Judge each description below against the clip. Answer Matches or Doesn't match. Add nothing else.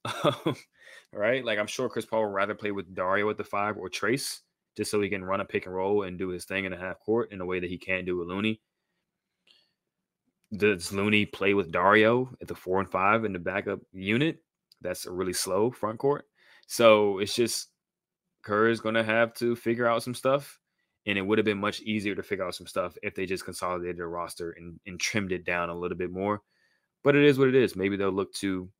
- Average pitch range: Matches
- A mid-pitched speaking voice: Doesn't match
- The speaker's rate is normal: Doesn't match